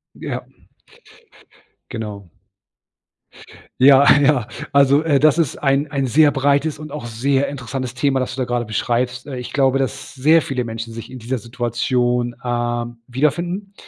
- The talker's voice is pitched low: Yes, low, 130 Hz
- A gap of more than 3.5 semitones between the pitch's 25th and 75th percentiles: No, average, 2.9 semitones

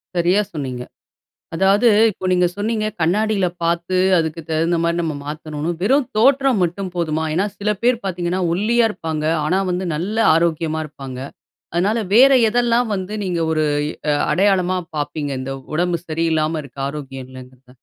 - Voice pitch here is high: No, medium, 175 Hz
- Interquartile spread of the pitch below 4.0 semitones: No, average, 4.7 semitones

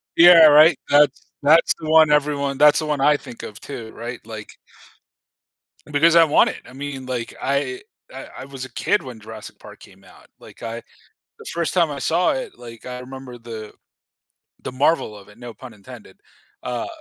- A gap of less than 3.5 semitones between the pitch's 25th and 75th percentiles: No, average, 4.1 semitones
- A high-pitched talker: No, low, 135 Hz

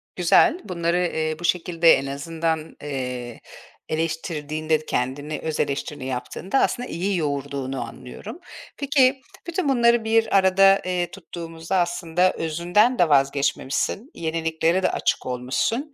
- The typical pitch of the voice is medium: Yes, medium, 165 Hz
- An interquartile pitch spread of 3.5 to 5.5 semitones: Yes, average, 4.7 semitones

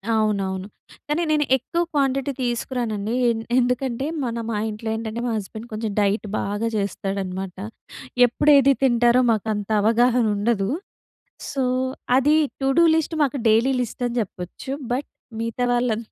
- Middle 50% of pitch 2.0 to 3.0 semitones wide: No, average, 3.6 semitones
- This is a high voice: Yes, high, 235 Hz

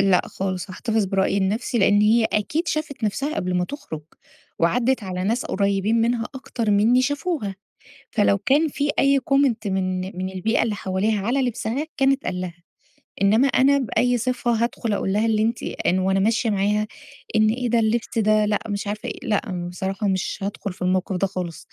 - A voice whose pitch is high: Yes, high, 215 Hz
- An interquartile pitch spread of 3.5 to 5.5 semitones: Yes, average, 4.1 semitones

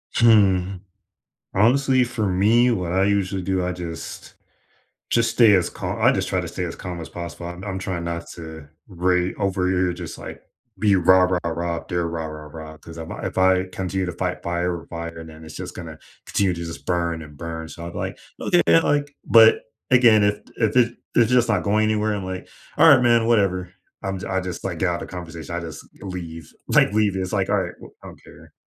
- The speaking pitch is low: Yes, very low, 90 Hz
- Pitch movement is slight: No, average, 3.3 semitones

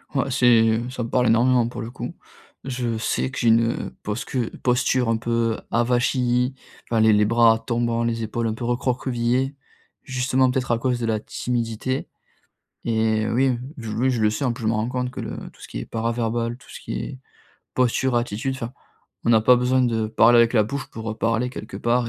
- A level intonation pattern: Yes, narrow, 1.8 semitones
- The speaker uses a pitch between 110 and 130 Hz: Yes, low, 120 Hz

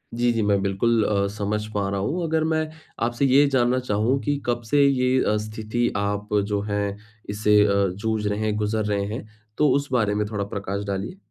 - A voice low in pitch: Yes, low, 105 Hz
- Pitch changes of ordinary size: Yes, average, 3.5 semitones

